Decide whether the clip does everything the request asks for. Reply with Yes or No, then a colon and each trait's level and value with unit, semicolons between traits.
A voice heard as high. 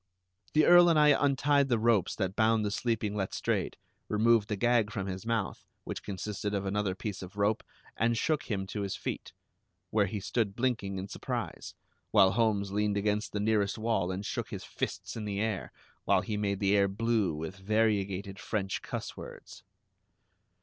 No: low, 105 Hz